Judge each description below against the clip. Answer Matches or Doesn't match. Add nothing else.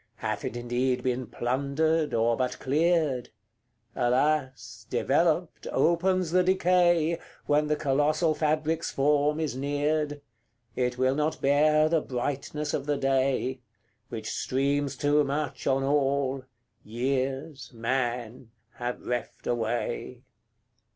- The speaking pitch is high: Doesn't match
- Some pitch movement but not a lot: Matches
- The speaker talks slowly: Matches